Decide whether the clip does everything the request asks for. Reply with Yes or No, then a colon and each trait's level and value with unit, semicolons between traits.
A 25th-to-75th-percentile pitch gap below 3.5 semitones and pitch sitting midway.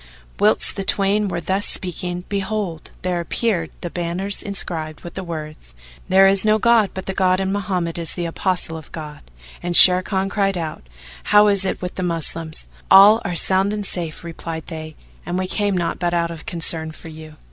Yes: average, 2.8 semitones; medium, 180 Hz